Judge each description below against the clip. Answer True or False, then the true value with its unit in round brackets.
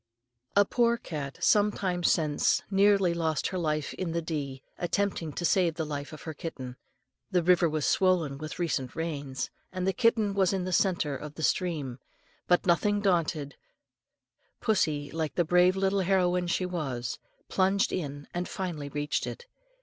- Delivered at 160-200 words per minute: True (165 wpm)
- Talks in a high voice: False (170 Hz)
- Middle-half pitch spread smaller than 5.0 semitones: True (3.9 semitones)